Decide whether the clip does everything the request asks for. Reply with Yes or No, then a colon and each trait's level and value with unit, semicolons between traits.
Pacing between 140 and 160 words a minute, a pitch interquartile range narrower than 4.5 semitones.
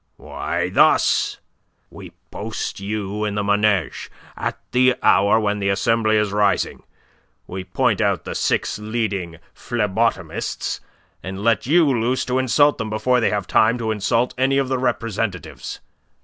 Yes: average, 150 wpm; average, 3.4 semitones